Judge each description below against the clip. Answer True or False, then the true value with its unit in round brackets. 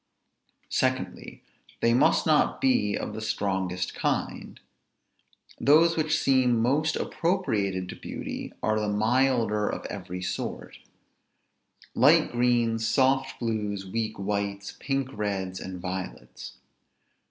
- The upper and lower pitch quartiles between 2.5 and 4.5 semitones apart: False (5.0 semitones)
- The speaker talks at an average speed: False (110 wpm)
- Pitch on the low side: True (110 Hz)